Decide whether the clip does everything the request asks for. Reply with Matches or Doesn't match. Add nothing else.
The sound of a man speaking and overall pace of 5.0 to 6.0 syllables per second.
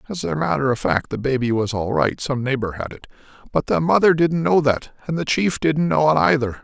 Matches